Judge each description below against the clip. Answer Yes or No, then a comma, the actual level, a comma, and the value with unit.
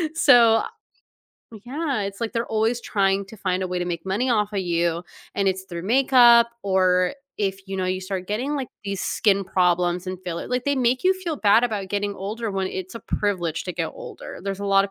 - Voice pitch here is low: No, high, 200 Hz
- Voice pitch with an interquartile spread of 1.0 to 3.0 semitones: No, average, 3.8 semitones